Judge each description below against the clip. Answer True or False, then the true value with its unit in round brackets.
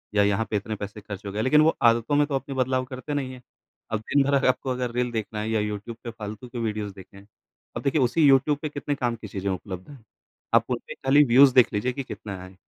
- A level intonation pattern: False (4.2 semitones)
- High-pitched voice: False (120 Hz)